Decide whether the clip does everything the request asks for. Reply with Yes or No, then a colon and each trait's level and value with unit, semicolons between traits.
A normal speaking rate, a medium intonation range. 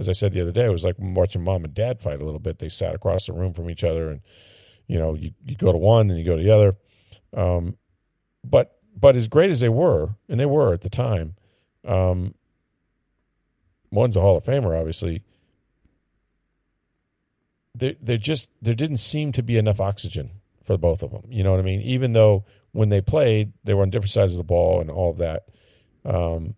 No: fast, 220 wpm; average, 4.0 semitones